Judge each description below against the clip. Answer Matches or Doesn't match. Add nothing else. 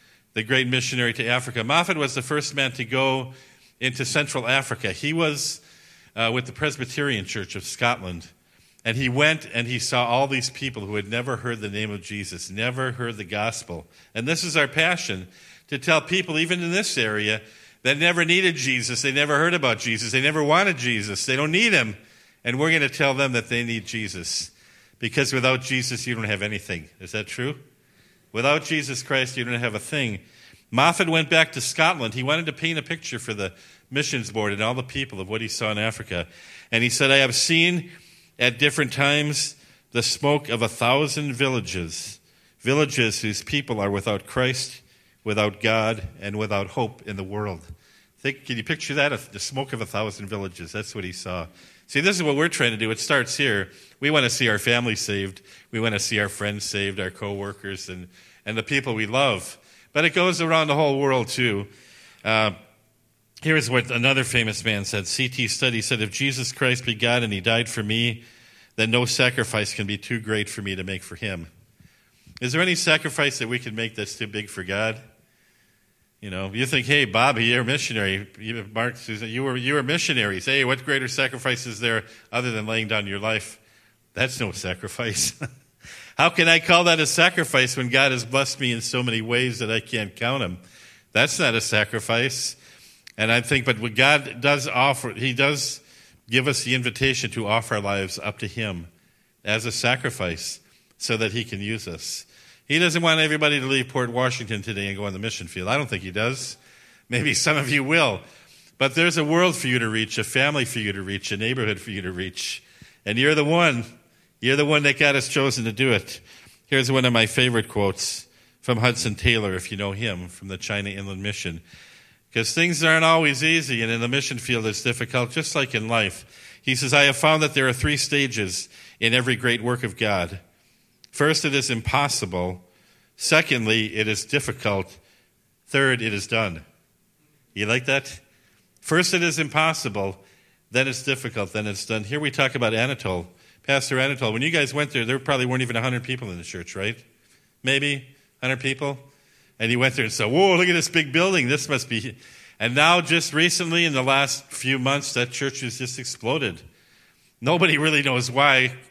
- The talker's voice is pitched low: Matches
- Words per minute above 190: Matches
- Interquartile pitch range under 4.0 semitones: Doesn't match